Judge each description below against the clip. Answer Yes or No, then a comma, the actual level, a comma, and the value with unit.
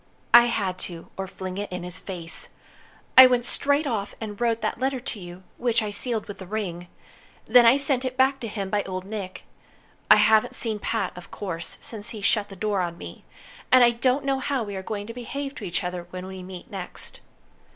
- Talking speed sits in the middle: No, fast, 220 wpm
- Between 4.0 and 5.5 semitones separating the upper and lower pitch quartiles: Yes, average, 4.5 semitones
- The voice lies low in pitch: No, high, 210 Hz